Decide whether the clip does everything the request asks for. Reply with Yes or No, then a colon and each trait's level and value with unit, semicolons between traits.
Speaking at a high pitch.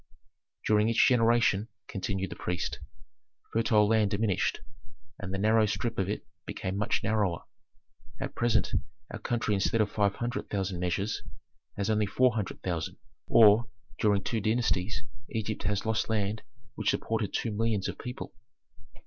No: low, 105 Hz